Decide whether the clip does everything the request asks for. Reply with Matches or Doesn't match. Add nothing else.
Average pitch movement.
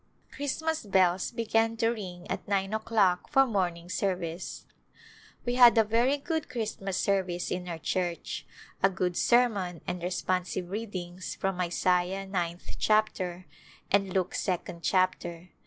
Matches